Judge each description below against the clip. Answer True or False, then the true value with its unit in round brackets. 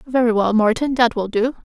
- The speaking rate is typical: False (210 wpm)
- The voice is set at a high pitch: True (235 Hz)